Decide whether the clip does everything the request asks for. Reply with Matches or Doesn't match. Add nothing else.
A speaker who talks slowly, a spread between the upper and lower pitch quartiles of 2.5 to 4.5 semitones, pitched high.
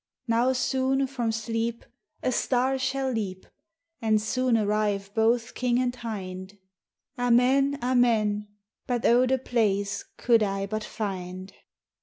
Matches